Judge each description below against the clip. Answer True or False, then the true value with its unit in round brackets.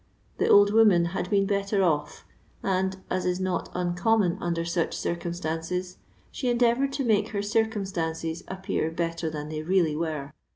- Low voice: False (180 Hz)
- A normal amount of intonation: True (3.4 semitones)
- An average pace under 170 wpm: True (160 wpm)